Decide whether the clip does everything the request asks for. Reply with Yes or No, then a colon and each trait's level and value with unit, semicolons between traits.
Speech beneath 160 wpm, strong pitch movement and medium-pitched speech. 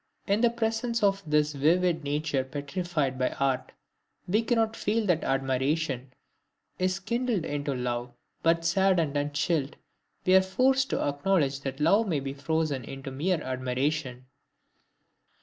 Yes: average, 140 wpm; wide, 5.8 semitones; medium, 155 Hz